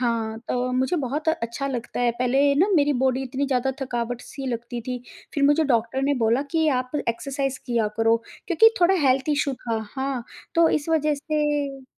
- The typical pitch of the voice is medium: No, very high, 265 Hz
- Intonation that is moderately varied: Yes, average, 3.0 semitones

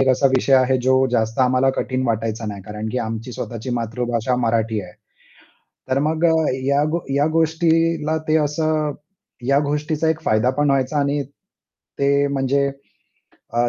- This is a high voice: No, low, 135 Hz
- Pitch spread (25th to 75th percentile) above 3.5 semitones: Yes, average, 4.2 semitones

